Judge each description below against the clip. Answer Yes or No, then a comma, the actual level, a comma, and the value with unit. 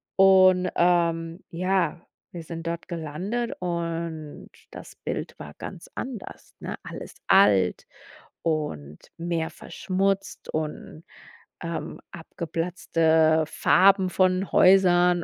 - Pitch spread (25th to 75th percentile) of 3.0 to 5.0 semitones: No, narrow, 2.4 semitones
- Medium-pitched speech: Yes, medium, 170 Hz